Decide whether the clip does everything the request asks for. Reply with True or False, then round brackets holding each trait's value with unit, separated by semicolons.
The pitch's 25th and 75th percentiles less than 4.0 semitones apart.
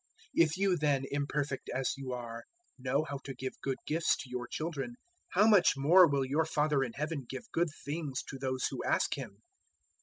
True (3.3 semitones)